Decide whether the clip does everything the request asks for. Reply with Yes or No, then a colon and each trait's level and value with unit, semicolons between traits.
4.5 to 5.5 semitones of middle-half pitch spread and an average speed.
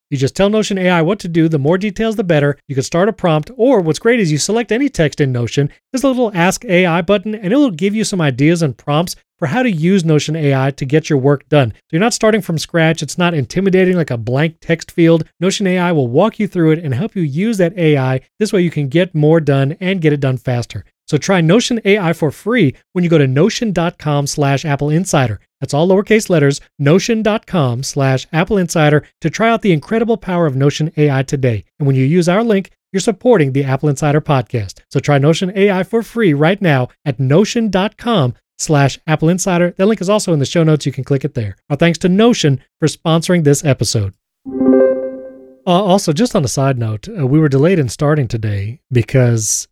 No: average, 5.2 semitones; fast, 225 wpm